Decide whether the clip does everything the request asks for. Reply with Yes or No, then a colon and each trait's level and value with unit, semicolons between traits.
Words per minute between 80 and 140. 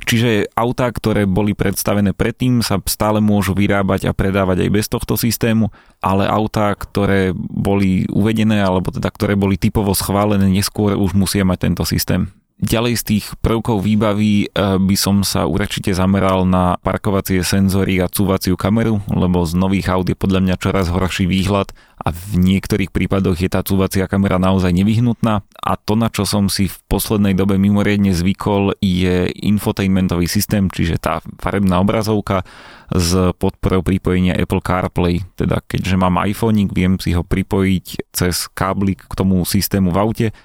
No: average, 160 wpm